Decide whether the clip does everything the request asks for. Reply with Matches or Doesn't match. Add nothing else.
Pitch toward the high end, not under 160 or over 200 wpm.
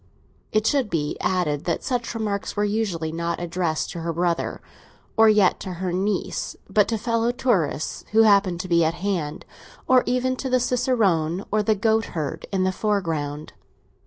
Matches